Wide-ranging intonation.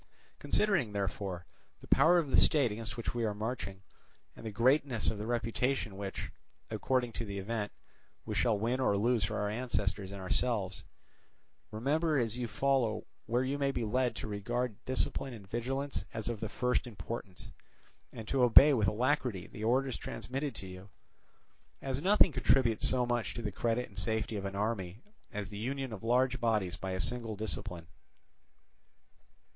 No: average, 3.8 semitones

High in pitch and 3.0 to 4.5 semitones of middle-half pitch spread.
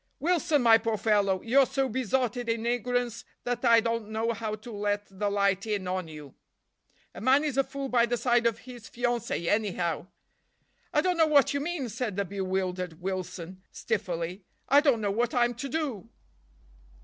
Yes: high, 230 Hz; average, 4.0 semitones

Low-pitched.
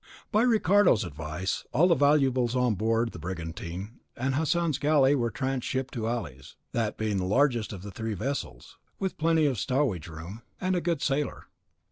Yes: low, 125 Hz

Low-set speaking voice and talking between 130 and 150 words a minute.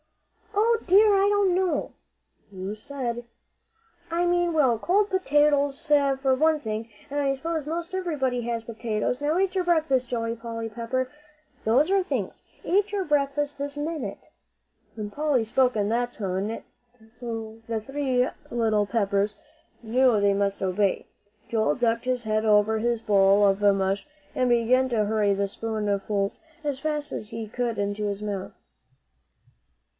No: high, 240 Hz; average, 145 wpm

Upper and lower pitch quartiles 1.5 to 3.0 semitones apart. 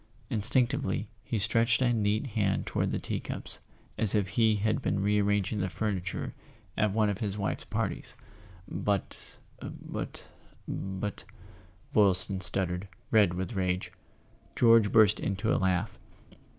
Yes: narrow, 2.4 semitones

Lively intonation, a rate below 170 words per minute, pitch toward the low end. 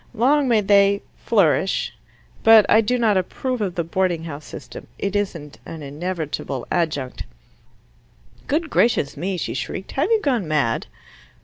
No: wide, 6.5 semitones; average, 150 wpm; high, 190 Hz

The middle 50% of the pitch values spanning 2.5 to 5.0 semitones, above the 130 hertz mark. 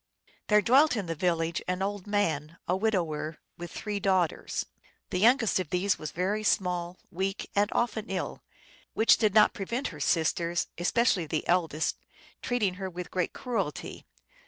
Yes: average, 3.5 semitones; medium, 185 Hz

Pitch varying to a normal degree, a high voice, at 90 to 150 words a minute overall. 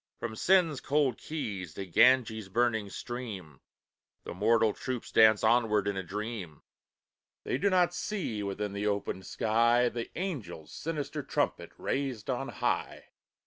No: average, 4.5 semitones; low, 110 Hz; average, 140 wpm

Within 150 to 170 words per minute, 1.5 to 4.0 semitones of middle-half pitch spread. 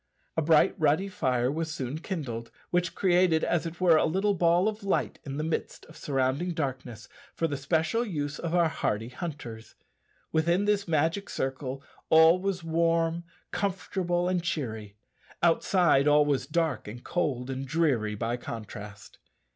No: average, 155 wpm; average, 4.7 semitones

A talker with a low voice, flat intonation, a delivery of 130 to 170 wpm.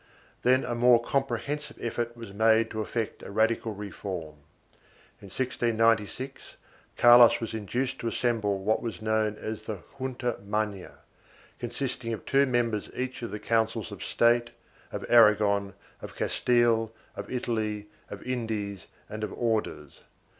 Yes: low, 115 Hz; narrow, 2.2 semitones; average, 140 wpm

